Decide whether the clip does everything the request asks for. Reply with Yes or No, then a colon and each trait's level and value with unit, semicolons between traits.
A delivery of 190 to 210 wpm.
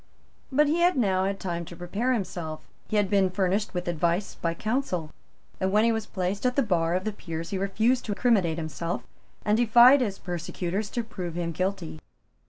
Yes: average, 195 wpm